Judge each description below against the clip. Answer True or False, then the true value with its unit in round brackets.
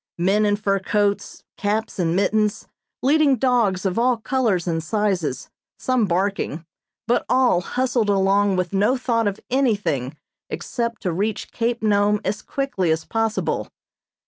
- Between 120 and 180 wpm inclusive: True (145 wpm)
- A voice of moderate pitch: False (205 Hz)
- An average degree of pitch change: True (3.6 semitones)